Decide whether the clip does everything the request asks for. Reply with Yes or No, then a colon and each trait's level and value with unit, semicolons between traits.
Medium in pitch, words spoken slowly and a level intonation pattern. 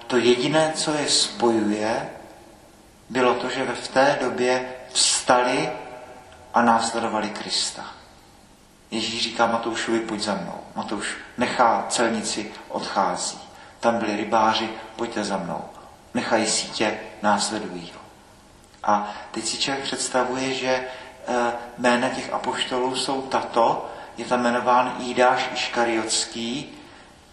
No: low, 120 Hz; slow, 110 wpm; narrow, 1.8 semitones